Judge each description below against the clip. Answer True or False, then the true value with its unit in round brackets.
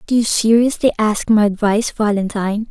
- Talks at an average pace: True (155 wpm)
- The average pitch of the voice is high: True (215 Hz)